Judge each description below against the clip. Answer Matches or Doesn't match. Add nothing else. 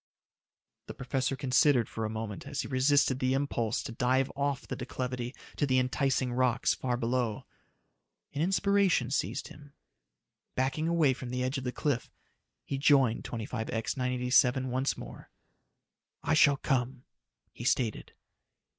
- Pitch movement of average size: Doesn't match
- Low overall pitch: Matches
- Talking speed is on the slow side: Doesn't match